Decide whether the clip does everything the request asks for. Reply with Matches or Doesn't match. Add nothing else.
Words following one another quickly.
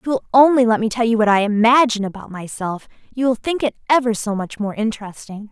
Matches